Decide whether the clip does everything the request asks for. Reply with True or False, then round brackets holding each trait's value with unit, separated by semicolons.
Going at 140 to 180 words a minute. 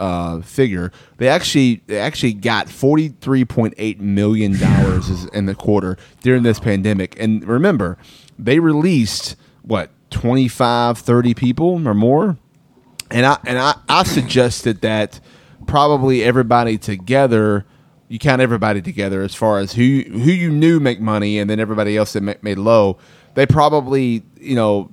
True (150 wpm)